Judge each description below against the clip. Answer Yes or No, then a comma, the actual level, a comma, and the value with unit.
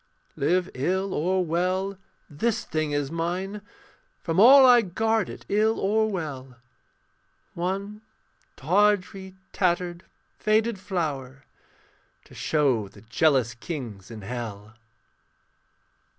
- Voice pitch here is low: No, medium, 175 Hz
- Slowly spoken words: Yes, slow, 105 wpm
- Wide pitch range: Yes, wide, 6.4 semitones